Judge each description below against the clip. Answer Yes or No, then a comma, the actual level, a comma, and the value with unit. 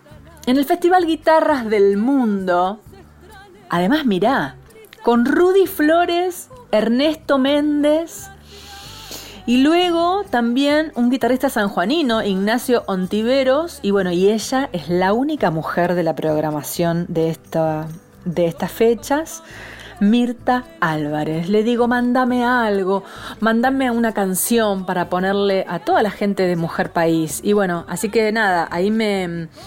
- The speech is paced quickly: No, slow, 125 wpm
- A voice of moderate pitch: No, high, 220 Hz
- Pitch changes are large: Yes, wide, 6.8 semitones